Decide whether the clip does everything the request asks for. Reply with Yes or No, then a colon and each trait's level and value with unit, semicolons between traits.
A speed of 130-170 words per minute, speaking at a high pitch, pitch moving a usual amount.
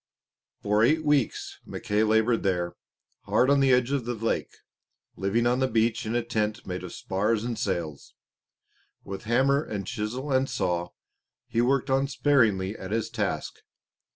No: average, 155 wpm; low, 115 Hz; average, 4.0 semitones